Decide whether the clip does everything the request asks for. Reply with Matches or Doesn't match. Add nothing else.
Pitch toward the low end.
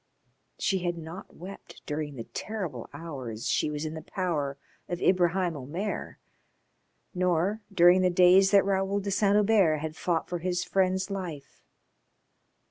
Doesn't match